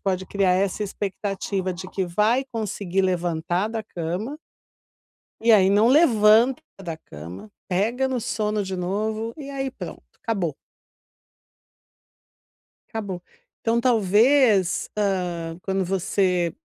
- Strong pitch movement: No, average, 3.6 semitones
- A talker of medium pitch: No, high, 200 Hz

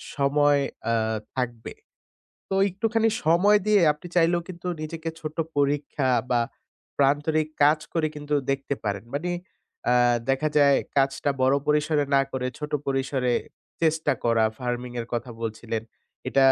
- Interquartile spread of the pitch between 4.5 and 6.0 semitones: No, average, 3.3 semitones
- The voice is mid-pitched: Yes, medium, 145 Hz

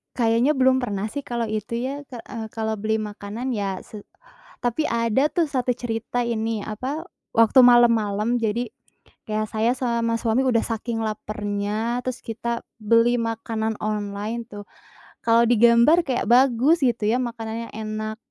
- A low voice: No, high, 230 Hz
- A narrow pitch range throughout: Yes, narrow, 2.1 semitones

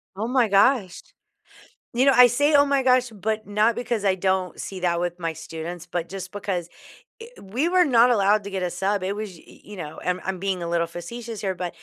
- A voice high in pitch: Yes, high, 195 Hz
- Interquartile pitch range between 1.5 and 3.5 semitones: No, average, 4.7 semitones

